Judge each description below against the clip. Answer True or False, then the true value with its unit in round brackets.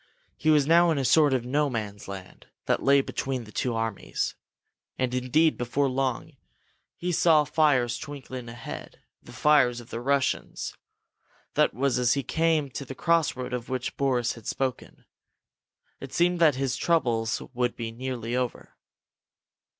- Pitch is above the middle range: False (130 Hz)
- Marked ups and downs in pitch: False (3.5 semitones)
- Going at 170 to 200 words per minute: False (160 wpm)